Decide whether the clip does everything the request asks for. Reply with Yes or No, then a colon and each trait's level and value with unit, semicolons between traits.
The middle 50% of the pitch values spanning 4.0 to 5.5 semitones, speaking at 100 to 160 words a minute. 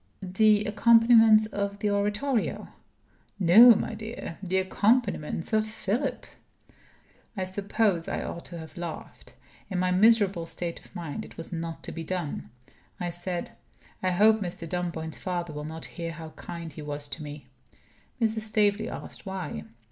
Yes: average, 4.4 semitones; average, 155 wpm